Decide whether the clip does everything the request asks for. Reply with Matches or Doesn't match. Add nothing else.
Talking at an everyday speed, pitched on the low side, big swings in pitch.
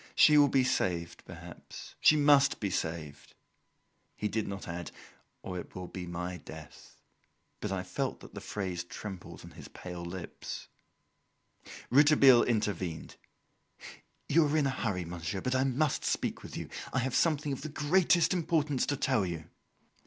Matches